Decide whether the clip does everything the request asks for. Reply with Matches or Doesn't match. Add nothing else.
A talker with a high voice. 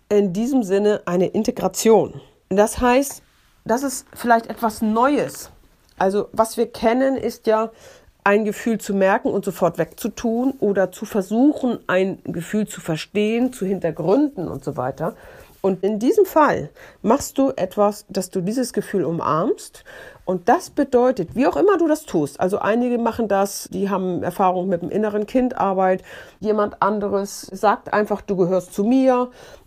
Matches